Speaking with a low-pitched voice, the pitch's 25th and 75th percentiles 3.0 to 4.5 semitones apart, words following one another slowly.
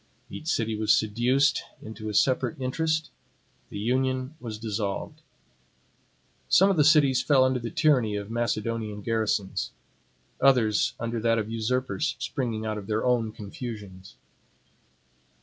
Yes: low, 115 Hz; average, 3.3 semitones; slow, 130 wpm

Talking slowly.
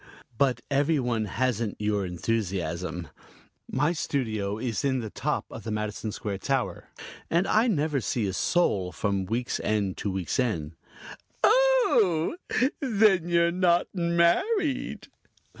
Yes: slow, 130 wpm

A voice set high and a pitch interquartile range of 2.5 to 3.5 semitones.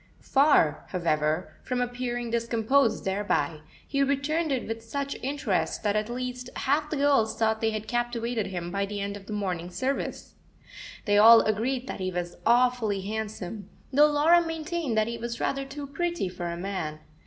No: high, 230 Hz; average, 5.3 semitones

